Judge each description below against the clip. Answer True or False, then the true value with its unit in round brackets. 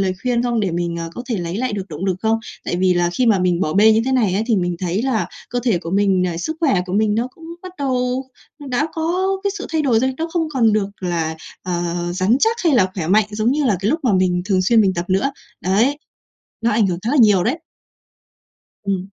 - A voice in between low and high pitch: False (210 Hz)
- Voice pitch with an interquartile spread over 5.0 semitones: True (5.5 semitones)